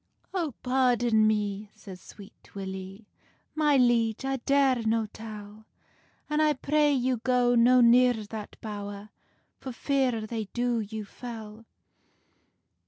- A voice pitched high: Yes, high, 230 Hz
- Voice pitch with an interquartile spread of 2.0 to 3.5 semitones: Yes, average, 3.1 semitones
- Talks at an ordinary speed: No, slow, 125 wpm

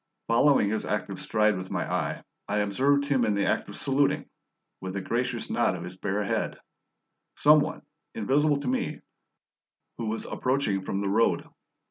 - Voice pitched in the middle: No, low, 115 Hz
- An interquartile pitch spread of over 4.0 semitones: Yes, average, 5.3 semitones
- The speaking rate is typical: Yes, average, 170 wpm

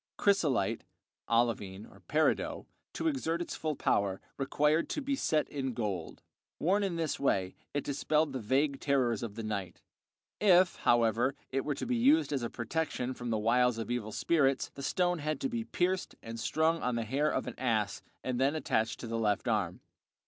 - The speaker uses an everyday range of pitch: No, wide, 5.7 semitones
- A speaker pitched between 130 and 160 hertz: Yes, low, 135 Hz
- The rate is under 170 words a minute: No, average, 185 wpm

